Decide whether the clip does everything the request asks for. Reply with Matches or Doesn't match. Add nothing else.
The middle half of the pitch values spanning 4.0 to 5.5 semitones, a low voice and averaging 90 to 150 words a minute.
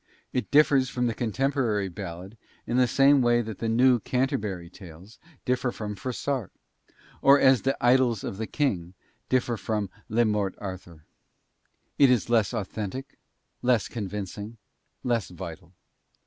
Matches